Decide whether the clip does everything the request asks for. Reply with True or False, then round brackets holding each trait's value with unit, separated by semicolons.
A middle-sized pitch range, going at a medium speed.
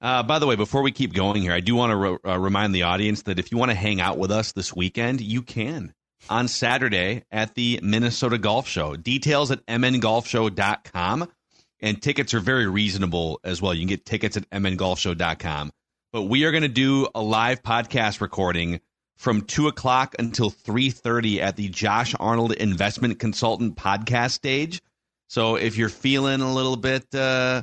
True (4.4 semitones; 185 wpm)